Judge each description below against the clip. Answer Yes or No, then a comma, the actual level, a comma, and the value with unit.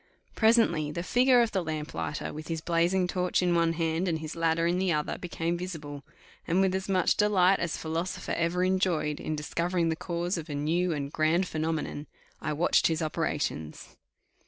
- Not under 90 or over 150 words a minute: No, average, 185 wpm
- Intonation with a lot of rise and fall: No, narrow, 2.5 semitones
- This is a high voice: No, medium, 170 Hz